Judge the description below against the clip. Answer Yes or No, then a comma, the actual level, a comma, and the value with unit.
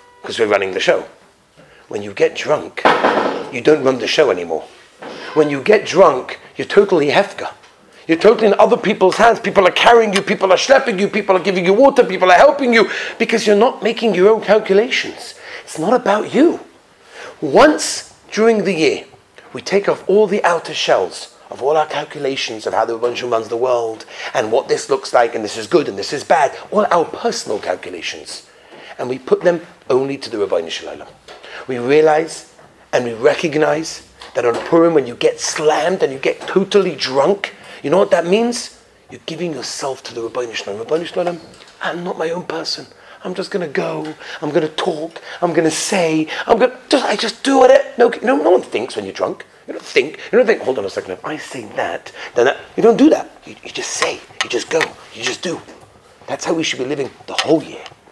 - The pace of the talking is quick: Yes, fast, 215 wpm